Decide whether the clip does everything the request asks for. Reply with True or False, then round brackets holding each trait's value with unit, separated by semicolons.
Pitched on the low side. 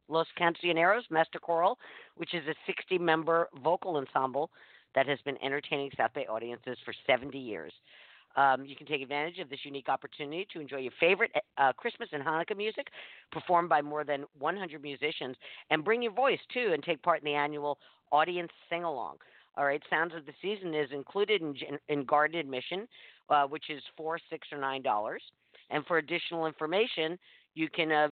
False (155 Hz)